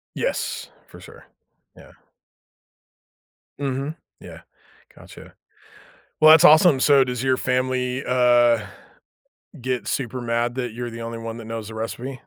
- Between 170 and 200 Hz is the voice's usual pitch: No, low, 125 Hz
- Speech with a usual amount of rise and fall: No, narrow, 2.2 semitones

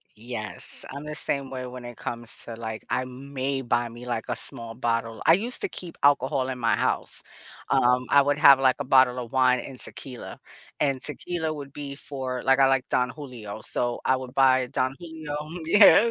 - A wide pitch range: No, narrow, 2.4 semitones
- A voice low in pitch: Yes, low, 130 Hz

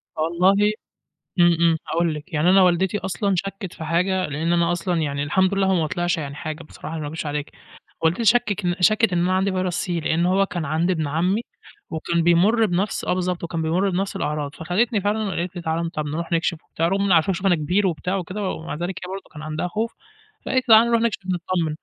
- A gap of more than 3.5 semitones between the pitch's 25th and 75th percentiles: No, average, 3.0 semitones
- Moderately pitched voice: Yes, medium, 175 Hz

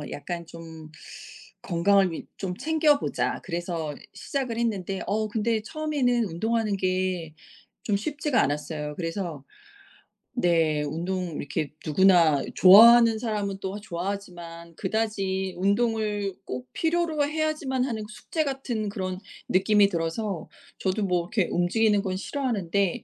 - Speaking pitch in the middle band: No, high, 195 Hz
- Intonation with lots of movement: No, average, 4.7 semitones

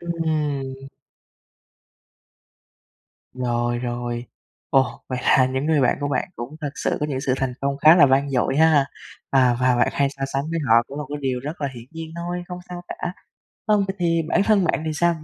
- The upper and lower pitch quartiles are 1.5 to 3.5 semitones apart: No, average, 4.0 semitones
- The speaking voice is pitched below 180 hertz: Yes, medium, 140 Hz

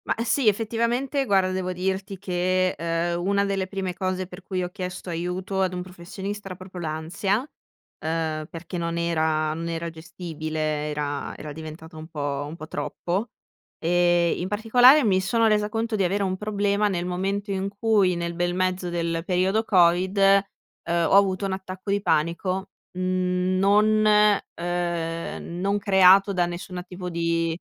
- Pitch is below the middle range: No, medium, 185 Hz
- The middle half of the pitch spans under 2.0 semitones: No, average, 2.7 semitones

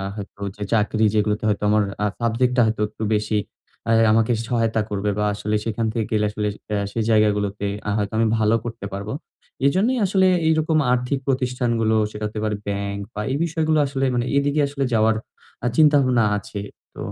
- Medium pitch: No, low, 110 Hz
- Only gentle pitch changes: No, average, 3.5 semitones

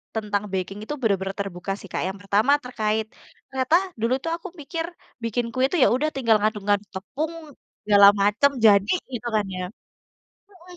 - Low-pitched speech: No, high, 215 Hz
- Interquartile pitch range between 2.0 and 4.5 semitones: No, average, 4.9 semitones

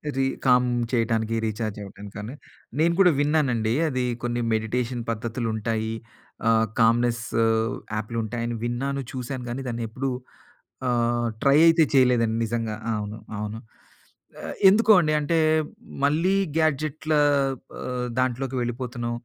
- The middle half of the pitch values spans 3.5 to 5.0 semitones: No, average, 3.0 semitones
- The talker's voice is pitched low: Yes, low, 120 Hz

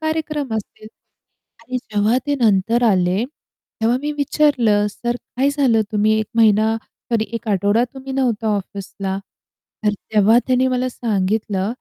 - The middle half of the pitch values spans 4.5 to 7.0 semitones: No, average, 3.6 semitones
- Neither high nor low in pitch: No, high, 225 Hz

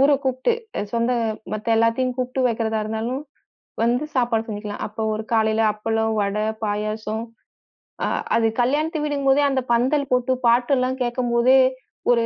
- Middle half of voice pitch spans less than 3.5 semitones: Yes, average, 2.7 semitones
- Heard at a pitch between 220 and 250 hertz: Yes, high, 235 Hz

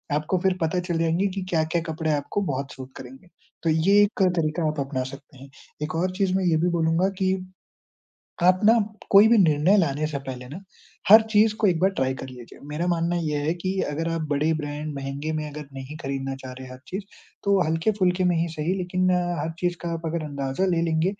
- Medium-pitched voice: Yes, medium, 165 Hz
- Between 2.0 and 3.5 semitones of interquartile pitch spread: No, average, 3.9 semitones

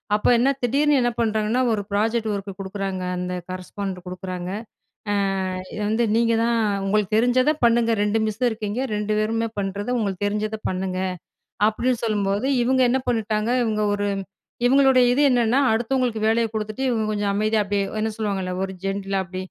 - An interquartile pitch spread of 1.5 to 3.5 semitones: Yes, average, 2.8 semitones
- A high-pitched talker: Yes, high, 215 Hz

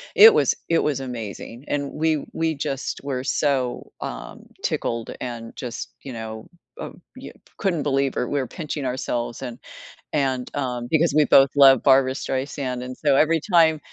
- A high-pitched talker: No, low, 135 Hz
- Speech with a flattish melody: No, average, 3.0 semitones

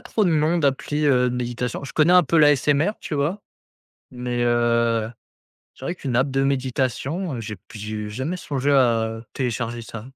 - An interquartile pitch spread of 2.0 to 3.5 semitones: No, average, 3.9 semitones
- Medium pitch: No, low, 130 Hz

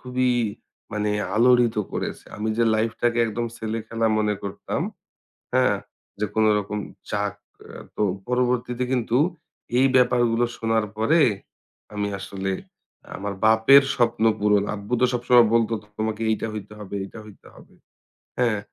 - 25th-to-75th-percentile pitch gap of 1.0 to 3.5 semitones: Yes, narrow, 2.4 semitones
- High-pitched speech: No, low, 115 Hz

